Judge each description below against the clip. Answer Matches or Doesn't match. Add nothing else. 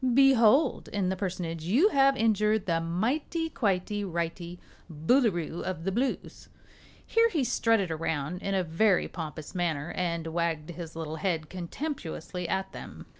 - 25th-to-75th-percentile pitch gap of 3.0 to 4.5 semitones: Doesn't match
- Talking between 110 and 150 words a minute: Matches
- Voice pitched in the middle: Matches